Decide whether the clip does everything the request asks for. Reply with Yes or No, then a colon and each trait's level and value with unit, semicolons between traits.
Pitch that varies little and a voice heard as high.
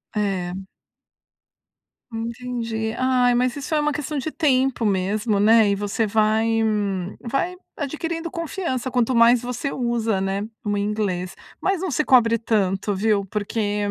No: average, 4.0 semitones; high, 230 Hz